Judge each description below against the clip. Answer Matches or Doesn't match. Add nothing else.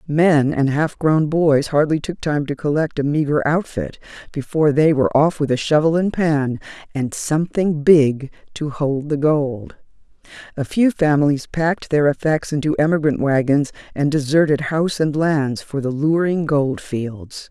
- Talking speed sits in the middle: Matches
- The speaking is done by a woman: Matches